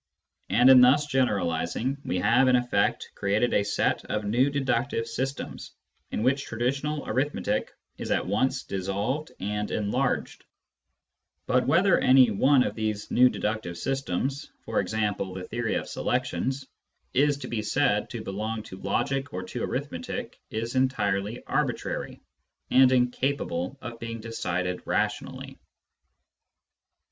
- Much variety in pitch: No, average, 4.4 semitones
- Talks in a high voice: No, low, 120 Hz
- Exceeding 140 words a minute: No, slow, 135 wpm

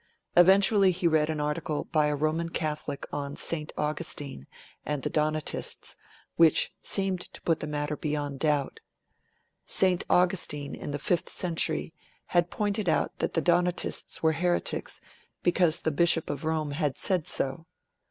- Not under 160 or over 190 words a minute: No, average, 150 wpm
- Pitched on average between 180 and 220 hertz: No, medium, 160 Hz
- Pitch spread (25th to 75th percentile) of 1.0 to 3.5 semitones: Yes, average, 2.8 semitones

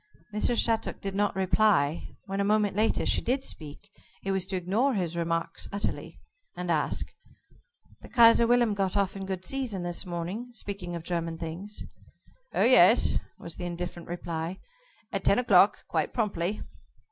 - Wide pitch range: No, average, 3.5 semitones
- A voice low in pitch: No, high, 190 Hz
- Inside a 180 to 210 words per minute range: No, average, 160 wpm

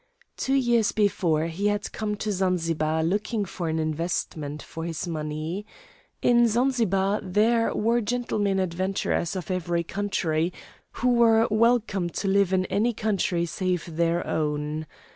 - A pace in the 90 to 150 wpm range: Yes, average, 140 wpm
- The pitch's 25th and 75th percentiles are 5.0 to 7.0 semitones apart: No, average, 4.5 semitones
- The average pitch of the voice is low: No, high, 190 Hz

